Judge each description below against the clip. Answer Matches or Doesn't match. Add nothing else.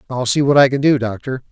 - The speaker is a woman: Doesn't match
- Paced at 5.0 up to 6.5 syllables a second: Matches